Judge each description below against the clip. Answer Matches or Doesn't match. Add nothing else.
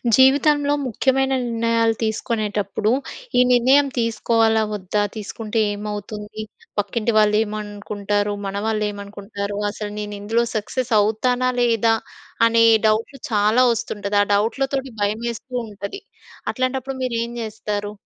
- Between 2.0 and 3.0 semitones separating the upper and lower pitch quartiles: Matches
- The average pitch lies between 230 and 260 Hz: Doesn't match